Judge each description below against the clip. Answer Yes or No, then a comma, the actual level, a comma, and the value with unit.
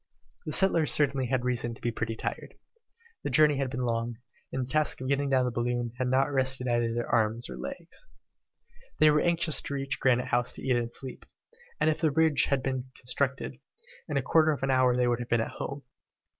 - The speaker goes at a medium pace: No, fast, 220 wpm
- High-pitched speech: No, low, 130 Hz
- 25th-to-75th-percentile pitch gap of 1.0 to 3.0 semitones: Yes, average, 2.7 semitones